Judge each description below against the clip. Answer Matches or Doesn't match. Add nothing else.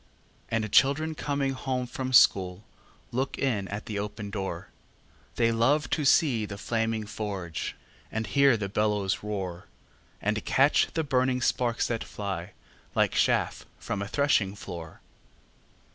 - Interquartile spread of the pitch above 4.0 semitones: Matches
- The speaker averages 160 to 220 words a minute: Doesn't match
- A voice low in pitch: Matches